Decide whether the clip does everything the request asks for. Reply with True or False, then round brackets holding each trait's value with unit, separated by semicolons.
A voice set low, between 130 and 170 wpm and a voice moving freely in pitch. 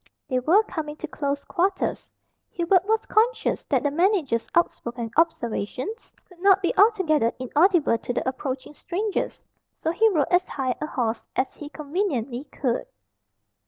False (310 Hz; 150 wpm; 6.6 semitones)